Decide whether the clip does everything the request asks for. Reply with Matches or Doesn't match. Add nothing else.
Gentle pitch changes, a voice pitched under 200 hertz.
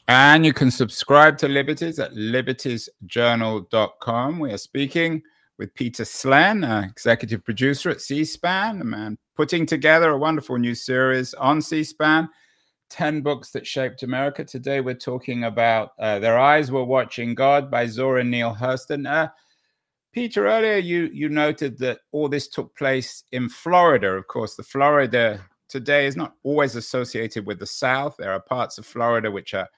Doesn't match